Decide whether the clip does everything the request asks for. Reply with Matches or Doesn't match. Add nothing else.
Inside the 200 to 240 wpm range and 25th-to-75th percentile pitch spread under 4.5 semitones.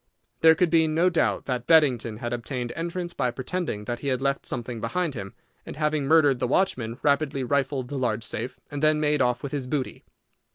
Matches